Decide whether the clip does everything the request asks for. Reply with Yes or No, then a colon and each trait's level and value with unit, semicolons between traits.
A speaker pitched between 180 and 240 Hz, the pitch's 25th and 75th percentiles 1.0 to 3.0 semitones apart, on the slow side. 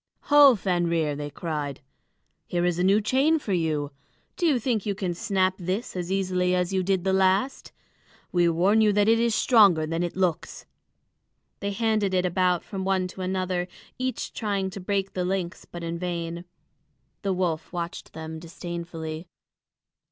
No: medium, 185 Hz; narrow, 2.6 semitones; average, 170 wpm